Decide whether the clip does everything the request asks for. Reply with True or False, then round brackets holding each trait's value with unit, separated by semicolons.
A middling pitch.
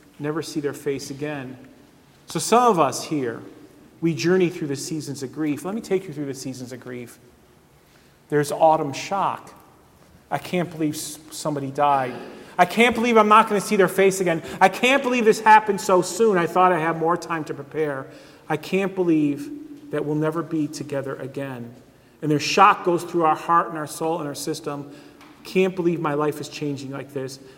True (155 Hz)